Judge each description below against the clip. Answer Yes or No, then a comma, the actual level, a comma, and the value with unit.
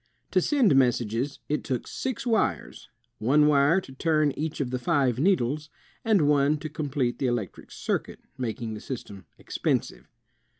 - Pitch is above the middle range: No, medium, 140 Hz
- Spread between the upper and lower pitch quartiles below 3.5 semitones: No, average, 3.9 semitones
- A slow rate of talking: No, average, 155 wpm